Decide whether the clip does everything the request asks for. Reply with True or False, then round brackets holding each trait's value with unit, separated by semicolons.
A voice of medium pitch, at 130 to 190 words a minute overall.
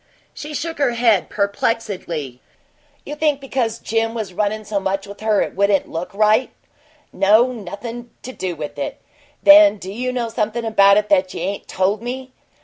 False (215 Hz; 180 wpm)